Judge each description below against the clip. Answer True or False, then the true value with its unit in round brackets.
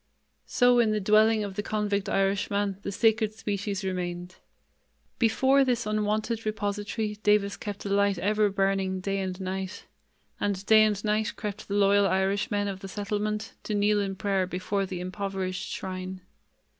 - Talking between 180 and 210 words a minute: False (155 wpm)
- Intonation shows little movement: True (1.7 semitones)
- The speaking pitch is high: True (205 Hz)